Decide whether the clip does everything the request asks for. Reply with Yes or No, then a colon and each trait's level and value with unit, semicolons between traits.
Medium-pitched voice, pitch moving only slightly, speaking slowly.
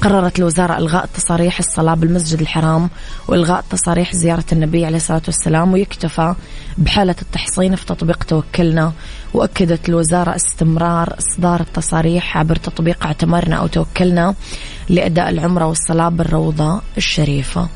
Yes: medium, 170 Hz; narrow, 1.6 semitones; slow, 120 wpm